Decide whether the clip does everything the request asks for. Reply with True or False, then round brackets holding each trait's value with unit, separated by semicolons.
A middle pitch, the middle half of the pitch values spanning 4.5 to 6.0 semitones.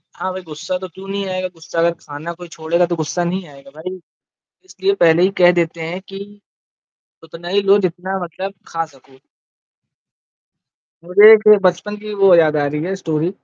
False (175 Hz; 2.9 semitones)